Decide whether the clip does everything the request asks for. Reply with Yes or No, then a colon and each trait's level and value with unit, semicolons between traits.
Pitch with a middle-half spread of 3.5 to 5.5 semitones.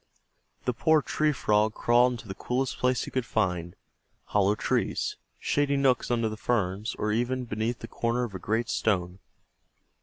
No: average, 3.1 semitones